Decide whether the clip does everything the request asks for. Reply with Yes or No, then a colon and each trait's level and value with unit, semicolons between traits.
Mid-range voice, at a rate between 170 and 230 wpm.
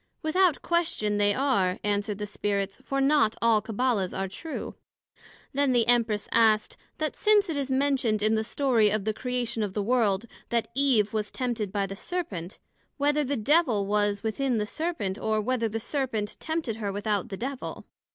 No: high, 225 Hz; average, 180 wpm